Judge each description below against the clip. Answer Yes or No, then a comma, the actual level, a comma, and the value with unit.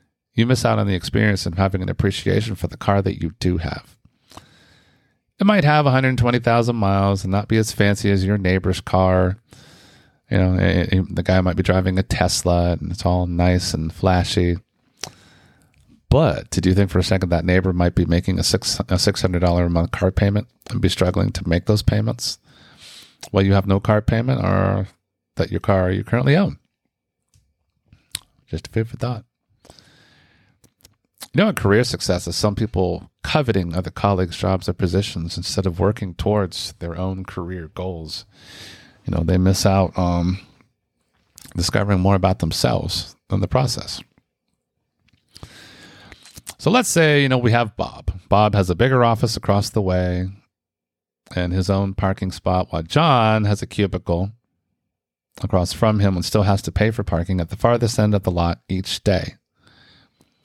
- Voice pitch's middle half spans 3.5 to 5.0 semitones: No, average, 2.8 semitones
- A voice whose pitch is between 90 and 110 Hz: Yes, very low, 95 Hz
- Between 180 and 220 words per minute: No, average, 170 wpm